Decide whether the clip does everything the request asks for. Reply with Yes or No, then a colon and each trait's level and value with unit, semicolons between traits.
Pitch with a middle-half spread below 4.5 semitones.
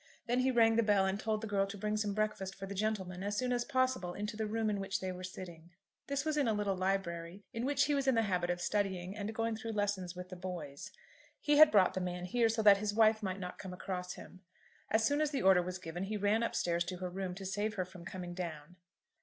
Yes: average, 3.3 semitones